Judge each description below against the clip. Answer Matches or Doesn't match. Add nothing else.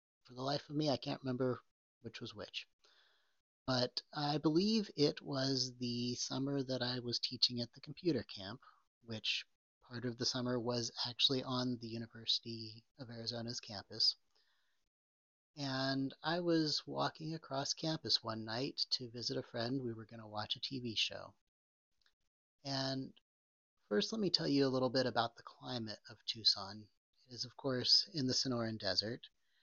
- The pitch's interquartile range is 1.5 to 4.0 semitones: Matches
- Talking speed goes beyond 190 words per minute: Doesn't match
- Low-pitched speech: Matches